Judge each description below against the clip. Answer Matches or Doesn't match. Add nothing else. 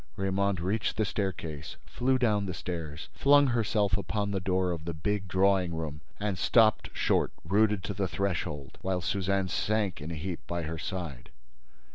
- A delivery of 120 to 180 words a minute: Matches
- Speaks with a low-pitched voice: Matches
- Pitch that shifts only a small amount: Doesn't match